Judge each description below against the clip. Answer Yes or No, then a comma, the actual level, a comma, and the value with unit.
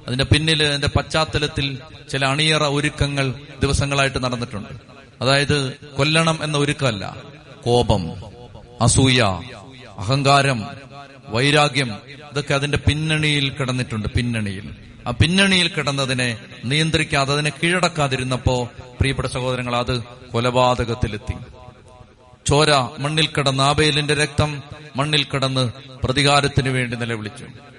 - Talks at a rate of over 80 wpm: Yes, average, 90 wpm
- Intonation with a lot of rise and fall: No, average, 2.9 semitones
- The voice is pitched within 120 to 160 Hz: Yes, low, 135 Hz